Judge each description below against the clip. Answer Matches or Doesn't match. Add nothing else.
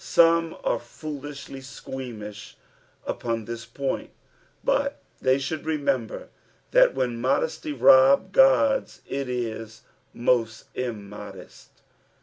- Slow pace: Matches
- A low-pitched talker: Matches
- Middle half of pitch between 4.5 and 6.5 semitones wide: Matches